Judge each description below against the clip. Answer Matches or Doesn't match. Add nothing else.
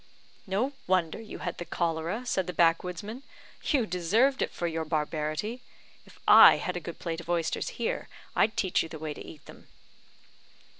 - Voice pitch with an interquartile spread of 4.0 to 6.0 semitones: Matches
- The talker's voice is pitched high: Doesn't match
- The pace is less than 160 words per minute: Doesn't match